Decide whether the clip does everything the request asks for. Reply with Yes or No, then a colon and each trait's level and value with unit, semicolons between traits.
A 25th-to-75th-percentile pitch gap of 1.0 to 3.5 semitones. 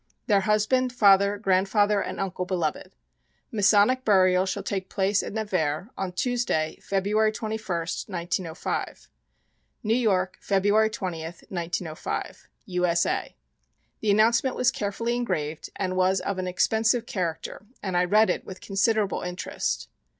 Yes: average, 3.0 semitones